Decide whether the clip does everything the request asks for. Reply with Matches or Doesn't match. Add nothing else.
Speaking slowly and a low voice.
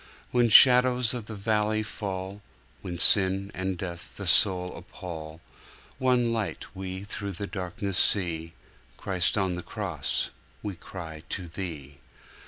Matches